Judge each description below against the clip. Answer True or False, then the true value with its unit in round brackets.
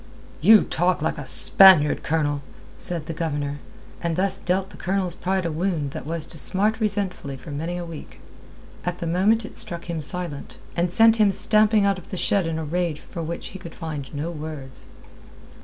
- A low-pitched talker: False (170 Hz)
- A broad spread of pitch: False (3.6 semitones)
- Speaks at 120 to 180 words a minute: False (195 wpm)